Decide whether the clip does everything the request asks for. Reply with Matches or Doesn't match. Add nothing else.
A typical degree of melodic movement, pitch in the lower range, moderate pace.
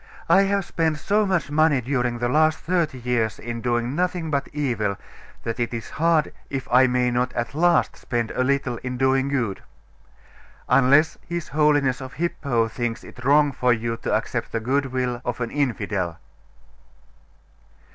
Matches